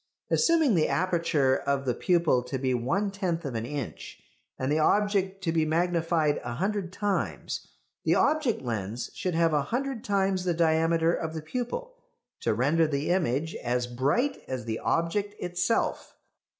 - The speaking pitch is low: No, medium, 165 Hz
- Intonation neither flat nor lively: No, wide, 5.9 semitones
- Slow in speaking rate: No, average, 165 wpm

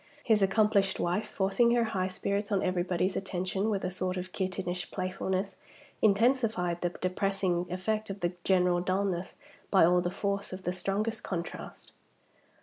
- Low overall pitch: No, high, 190 Hz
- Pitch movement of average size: No, narrow, 1.8 semitones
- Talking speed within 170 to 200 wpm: No, average, 150 wpm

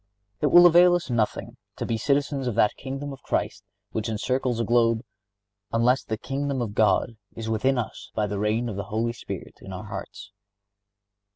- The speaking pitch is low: Yes, low, 115 Hz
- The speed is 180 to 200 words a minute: Yes, average, 185 wpm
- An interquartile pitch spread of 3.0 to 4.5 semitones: Yes, average, 3.7 semitones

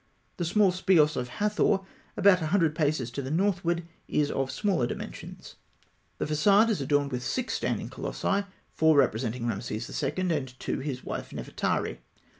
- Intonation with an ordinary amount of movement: No, wide, 6.5 semitones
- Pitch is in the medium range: Yes, medium, 155 Hz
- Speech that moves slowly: No, average, 160 wpm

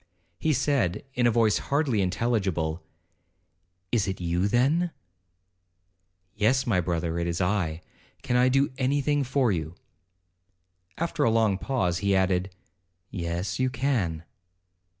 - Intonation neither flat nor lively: No, wide, 6.5 semitones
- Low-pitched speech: Yes, low, 105 Hz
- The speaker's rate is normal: No, slow, 130 wpm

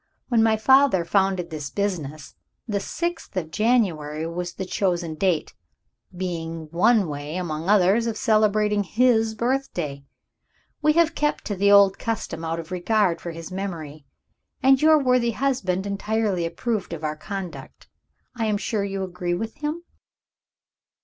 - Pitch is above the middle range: Yes, high, 195 Hz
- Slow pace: No, average, 150 wpm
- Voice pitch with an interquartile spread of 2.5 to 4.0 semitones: No, average, 4.9 semitones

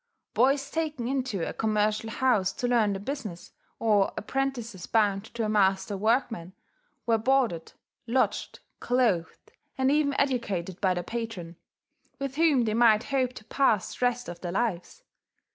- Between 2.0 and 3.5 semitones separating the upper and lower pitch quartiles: No, average, 4.8 semitones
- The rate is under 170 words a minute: Yes, average, 150 wpm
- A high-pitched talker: Yes, high, 225 Hz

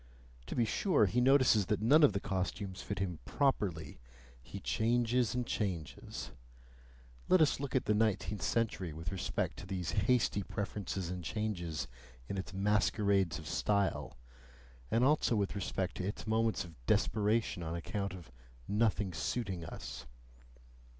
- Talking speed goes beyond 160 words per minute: No, average, 150 wpm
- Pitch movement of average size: Yes, average, 3.8 semitones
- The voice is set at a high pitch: No, low, 100 Hz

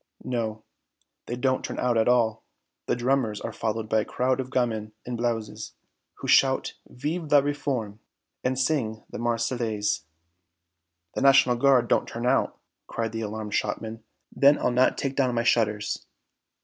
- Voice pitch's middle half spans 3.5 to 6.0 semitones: No, average, 2.8 semitones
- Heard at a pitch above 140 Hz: No, low, 120 Hz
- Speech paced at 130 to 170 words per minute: Yes, average, 160 wpm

